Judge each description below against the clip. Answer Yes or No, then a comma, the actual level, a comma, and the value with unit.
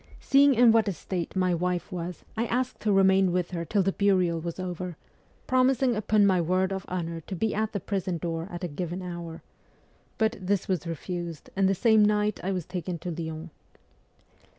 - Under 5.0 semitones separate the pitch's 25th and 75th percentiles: Yes, average, 3.2 semitones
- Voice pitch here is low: No, medium, 185 Hz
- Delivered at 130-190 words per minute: No, average, 200 wpm